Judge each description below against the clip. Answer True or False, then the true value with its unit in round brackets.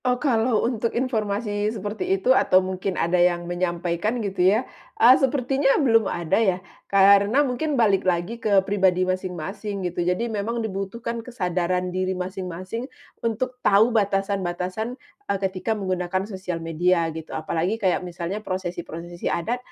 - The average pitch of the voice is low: False (195 Hz)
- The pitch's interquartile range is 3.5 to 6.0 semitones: True (3.8 semitones)